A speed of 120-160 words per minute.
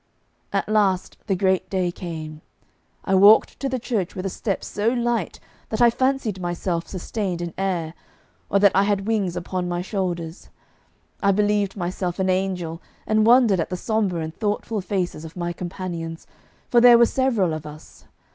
No: average, 175 wpm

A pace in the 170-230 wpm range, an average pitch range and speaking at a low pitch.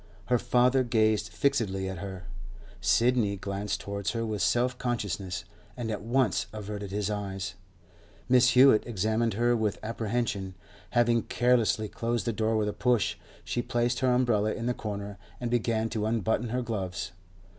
No: average, 155 wpm; average, 3.1 semitones; low, 110 Hz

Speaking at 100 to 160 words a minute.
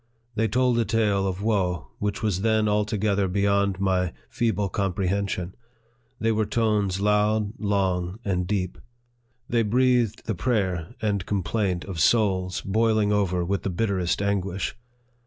Yes: average, 140 wpm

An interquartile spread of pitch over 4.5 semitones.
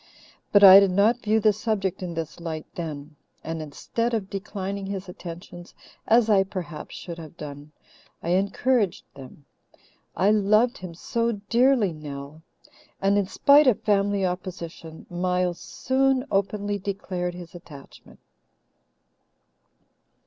No: average, 3.7 semitones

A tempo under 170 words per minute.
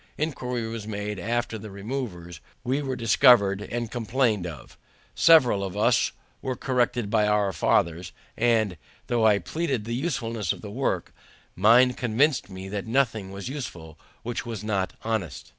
Yes: average, 155 wpm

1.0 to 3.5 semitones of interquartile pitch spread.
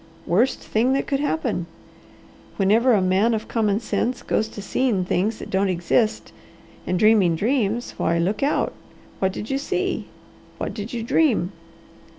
No: average, 4.4 semitones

